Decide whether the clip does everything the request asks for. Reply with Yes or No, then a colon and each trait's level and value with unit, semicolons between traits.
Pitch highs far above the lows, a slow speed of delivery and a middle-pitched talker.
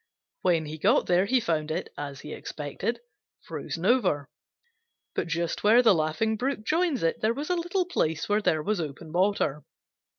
No: wide, 7.0 semitones; average, 175 wpm; medium, 180 Hz